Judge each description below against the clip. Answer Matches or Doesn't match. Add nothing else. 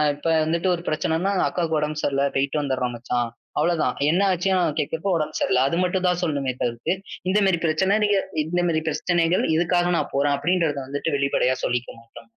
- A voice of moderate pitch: Matches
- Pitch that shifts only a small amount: Doesn't match